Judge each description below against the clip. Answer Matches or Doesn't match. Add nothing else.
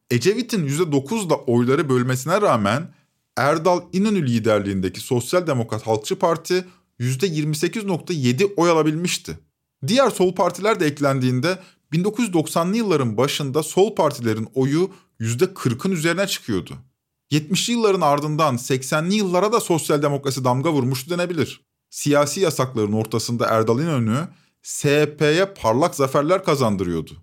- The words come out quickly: Doesn't match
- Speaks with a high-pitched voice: Doesn't match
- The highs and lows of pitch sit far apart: Matches